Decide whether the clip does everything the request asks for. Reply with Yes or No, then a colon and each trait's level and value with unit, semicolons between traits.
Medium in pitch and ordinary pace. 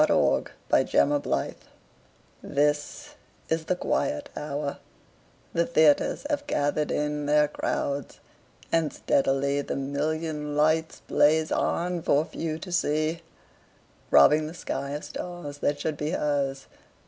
No: medium, 150 Hz; slow, 125 wpm